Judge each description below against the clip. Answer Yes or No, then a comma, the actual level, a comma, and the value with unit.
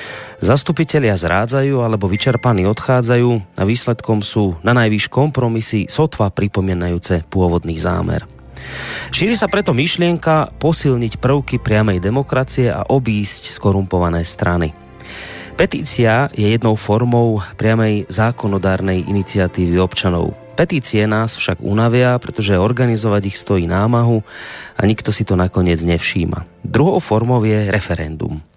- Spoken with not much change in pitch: No, average, 5.0 semitones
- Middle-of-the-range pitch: No, low, 110 Hz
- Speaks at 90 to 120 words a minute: Yes, average, 115 wpm